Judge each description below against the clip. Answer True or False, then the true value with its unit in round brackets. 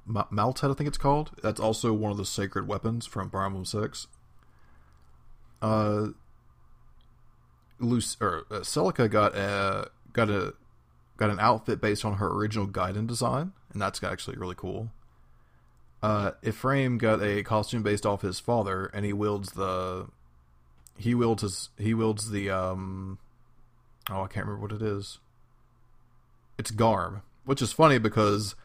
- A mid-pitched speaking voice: False (105 Hz)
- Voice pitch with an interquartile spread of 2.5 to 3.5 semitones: True (3.1 semitones)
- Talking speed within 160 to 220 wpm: False (150 wpm)